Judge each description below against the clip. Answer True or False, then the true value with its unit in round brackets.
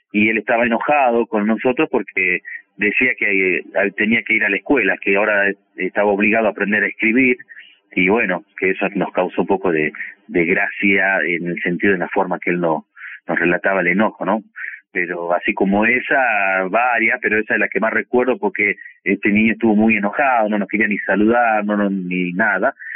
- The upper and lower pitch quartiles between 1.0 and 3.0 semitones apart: True (2.5 semitones)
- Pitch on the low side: True (105 Hz)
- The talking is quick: True (195 wpm)